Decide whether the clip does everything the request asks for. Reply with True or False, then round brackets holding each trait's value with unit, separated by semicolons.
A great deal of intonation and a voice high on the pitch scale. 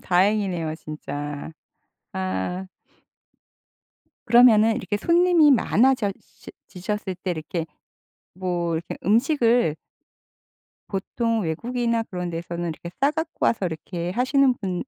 True (5.9 semitones; 195 Hz)